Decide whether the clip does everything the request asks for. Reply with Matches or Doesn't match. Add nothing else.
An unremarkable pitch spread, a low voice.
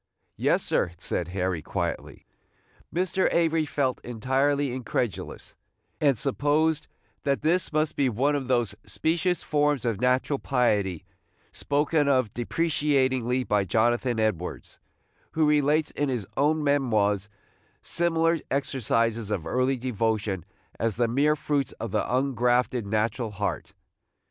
Matches